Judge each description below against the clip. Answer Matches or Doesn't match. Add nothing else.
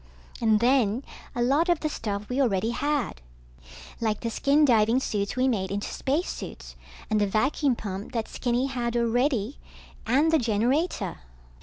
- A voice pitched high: Matches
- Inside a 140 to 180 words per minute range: Matches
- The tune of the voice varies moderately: Matches